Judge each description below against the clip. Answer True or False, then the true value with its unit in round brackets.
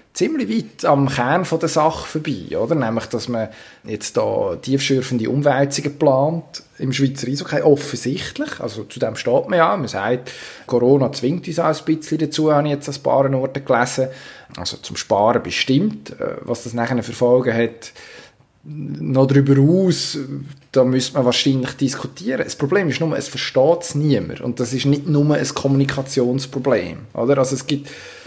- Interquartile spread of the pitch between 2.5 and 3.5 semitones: True (2.9 semitones)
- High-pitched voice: False (140 Hz)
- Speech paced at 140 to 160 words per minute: False (170 wpm)